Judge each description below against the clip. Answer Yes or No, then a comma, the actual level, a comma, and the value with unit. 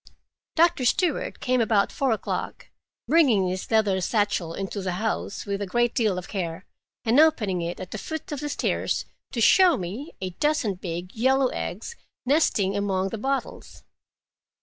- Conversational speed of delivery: Yes, average, 165 wpm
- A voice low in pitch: No, high, 215 Hz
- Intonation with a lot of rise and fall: Yes, wide, 6.1 semitones